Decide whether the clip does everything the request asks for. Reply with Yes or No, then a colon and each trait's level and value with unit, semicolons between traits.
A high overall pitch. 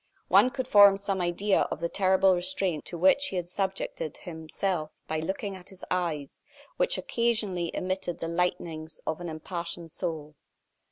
No: medium, 180 Hz